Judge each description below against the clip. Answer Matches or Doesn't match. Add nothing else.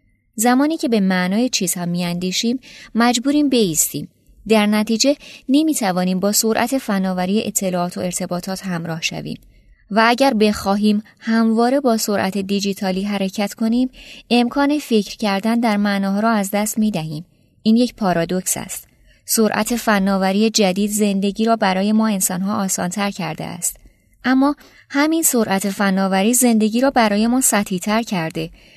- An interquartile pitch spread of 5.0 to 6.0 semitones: Doesn't match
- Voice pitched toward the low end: Doesn't match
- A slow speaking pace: Doesn't match